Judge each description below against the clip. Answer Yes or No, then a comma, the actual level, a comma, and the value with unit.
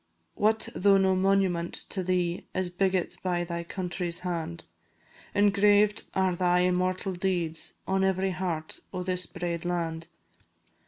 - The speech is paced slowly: Yes, slow, 130 wpm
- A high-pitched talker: No, medium, 180 Hz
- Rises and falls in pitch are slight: Yes, narrow, 1.7 semitones